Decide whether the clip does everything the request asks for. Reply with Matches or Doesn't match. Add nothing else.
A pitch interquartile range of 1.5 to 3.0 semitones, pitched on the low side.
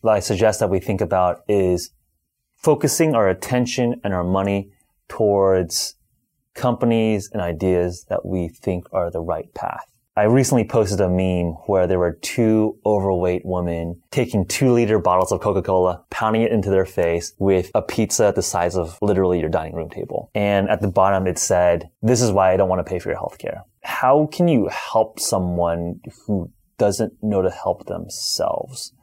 Doesn't match